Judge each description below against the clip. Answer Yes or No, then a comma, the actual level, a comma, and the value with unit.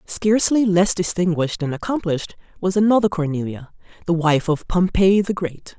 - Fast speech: No, average, 145 wpm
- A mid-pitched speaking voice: Yes, medium, 180 Hz